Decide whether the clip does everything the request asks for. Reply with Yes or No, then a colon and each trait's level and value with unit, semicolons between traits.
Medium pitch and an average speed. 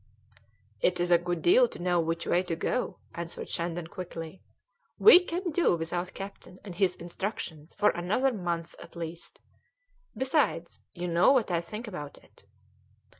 Yes: medium, 175 Hz; average, 165 wpm